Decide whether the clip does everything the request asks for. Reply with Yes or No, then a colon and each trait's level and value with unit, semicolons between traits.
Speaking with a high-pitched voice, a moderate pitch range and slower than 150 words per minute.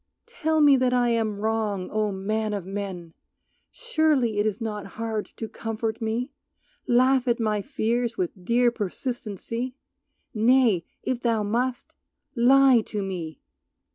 Yes: high, 225 Hz; average, 3.1 semitones; average, 140 wpm